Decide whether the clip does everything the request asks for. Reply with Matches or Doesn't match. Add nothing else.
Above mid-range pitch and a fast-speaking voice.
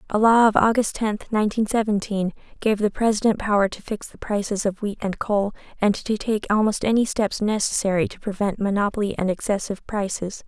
Doesn't match